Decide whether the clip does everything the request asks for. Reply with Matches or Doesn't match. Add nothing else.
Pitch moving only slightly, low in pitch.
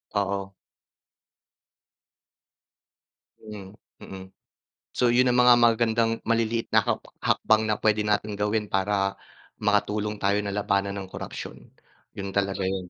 Matches